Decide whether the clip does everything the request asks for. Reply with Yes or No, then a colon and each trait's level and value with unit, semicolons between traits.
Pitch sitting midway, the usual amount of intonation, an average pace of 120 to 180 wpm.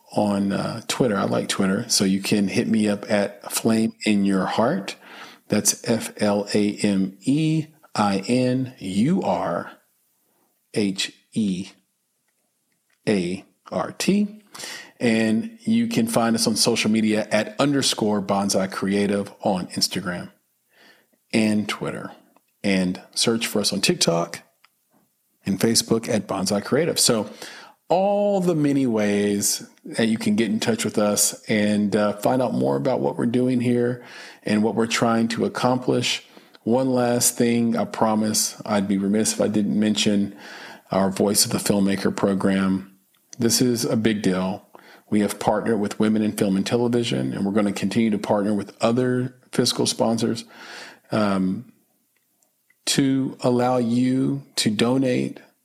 No: low, 110 Hz; average, 3.3 semitones; average, 150 wpm